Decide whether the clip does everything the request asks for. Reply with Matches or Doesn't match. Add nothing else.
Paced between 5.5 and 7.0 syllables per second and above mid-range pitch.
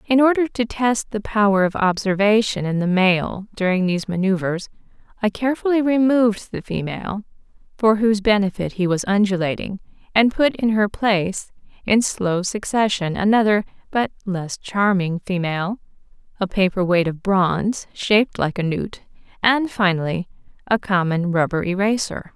Doesn't match